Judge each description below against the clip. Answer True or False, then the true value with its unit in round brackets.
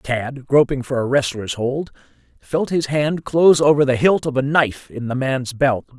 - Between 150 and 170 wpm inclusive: False (200 wpm)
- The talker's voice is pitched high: False (135 Hz)